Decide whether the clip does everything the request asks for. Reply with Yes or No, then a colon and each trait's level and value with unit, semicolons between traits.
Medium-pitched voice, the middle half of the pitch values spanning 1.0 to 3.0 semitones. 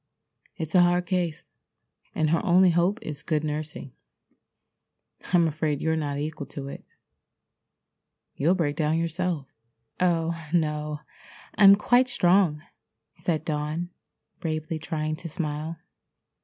Yes: medium, 160 Hz; narrow, 2.6 semitones